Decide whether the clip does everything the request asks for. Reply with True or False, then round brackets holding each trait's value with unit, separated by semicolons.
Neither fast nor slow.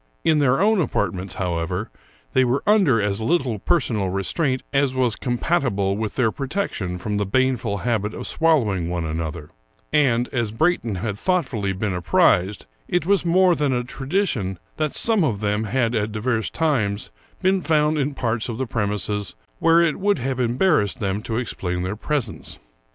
True (170 wpm)